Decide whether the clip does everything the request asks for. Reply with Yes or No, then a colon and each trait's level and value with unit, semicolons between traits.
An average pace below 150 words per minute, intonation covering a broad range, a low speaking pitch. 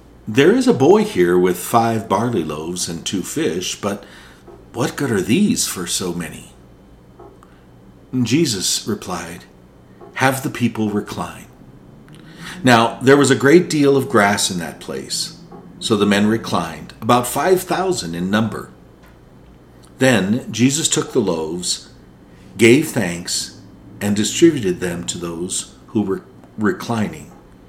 Yes: slow, 135 wpm; wide, 6.9 semitones; low, 105 Hz